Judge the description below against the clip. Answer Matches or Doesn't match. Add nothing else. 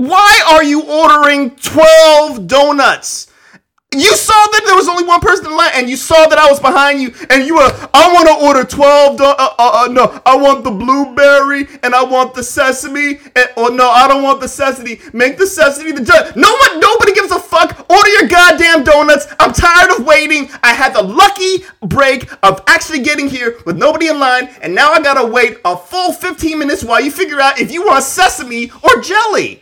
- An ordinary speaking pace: Doesn't match